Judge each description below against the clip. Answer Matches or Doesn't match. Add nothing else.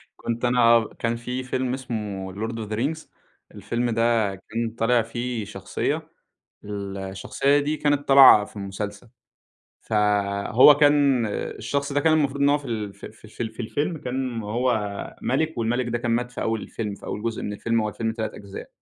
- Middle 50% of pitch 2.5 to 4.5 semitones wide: Matches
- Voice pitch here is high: Doesn't match